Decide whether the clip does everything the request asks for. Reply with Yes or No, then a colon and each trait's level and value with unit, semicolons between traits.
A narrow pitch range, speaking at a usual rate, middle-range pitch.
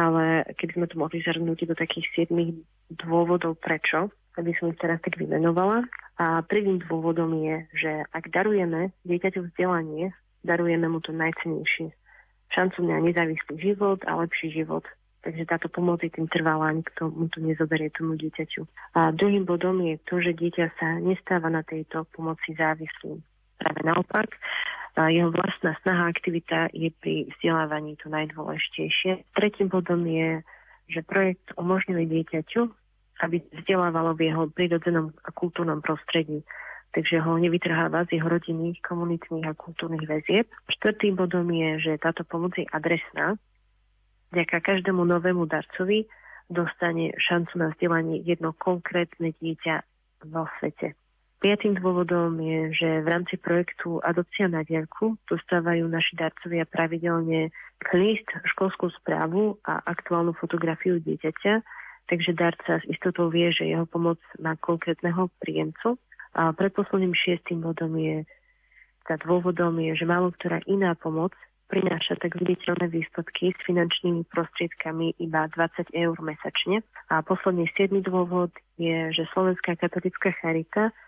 Yes: narrow, 1.8 semitones; average, 135 wpm; medium, 170 Hz